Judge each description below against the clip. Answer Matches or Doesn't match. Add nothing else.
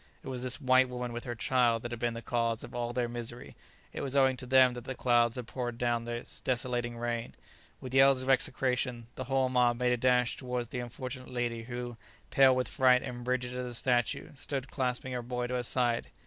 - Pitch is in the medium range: Doesn't match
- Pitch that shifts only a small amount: Matches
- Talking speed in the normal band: Doesn't match